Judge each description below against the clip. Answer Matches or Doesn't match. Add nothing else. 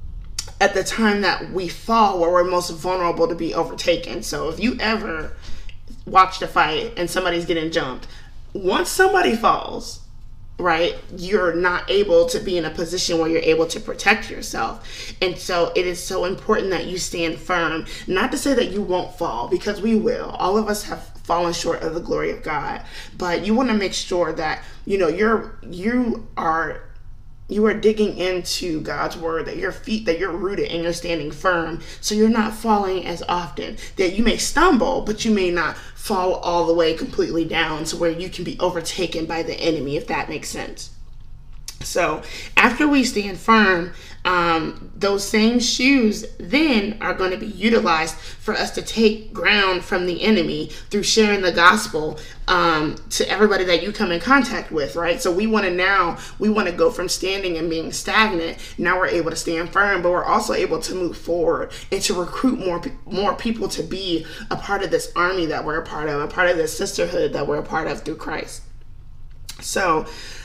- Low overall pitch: Doesn't match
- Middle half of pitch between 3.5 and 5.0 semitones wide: Matches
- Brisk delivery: Doesn't match